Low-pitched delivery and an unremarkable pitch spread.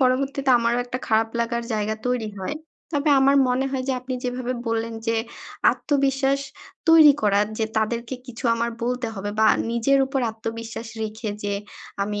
No: high, 235 Hz; average, 3.1 semitones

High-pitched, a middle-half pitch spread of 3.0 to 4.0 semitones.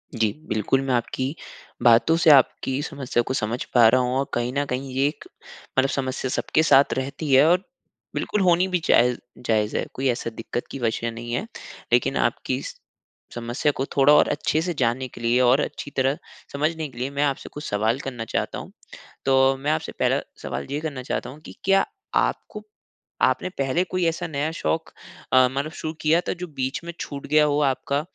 No: low, 135 Hz; average, 3.6 semitones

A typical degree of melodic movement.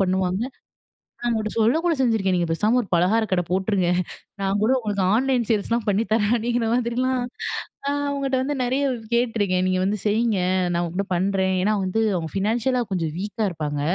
Yes: average, 4.1 semitones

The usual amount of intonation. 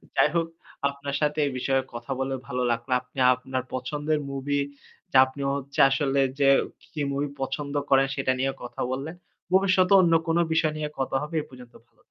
No: narrow, 2.2 semitones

